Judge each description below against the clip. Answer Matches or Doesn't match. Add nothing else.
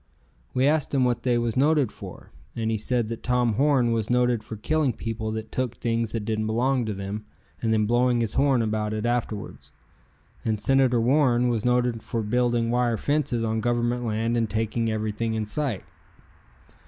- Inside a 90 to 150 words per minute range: Doesn't match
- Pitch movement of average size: Doesn't match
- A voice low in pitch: Matches